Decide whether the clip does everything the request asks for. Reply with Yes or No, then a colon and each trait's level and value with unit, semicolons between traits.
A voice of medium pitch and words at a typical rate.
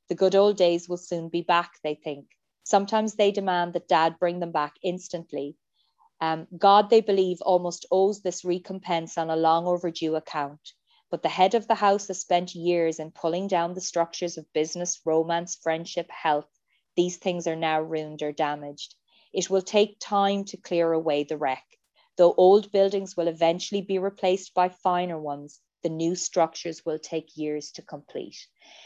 Yes: medium, 175 Hz; average, 175 wpm